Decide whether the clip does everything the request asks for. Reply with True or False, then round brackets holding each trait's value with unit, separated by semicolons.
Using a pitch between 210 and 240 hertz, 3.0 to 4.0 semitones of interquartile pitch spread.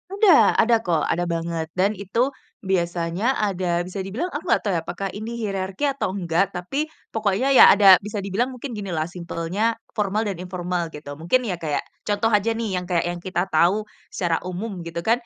False (190 Hz; 3.7 semitones)